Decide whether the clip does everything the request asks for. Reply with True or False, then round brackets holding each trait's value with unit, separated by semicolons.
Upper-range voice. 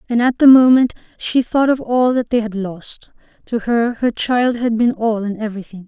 True (230 Hz)